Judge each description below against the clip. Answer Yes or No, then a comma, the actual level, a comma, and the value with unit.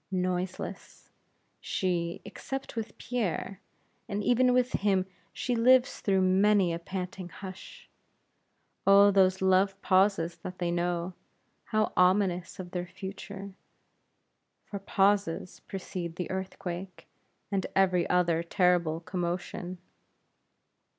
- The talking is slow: Yes, slow, 110 wpm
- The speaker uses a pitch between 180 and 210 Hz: Yes, medium, 185 Hz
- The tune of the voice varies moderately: No, narrow, 2.0 semitones